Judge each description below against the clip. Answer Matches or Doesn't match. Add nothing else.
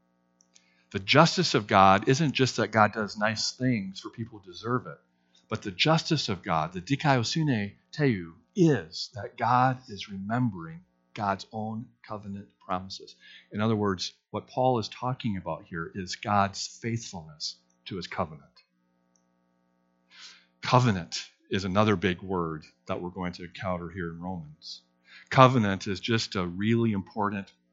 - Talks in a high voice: Doesn't match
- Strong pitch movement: Matches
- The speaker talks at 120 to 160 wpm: Matches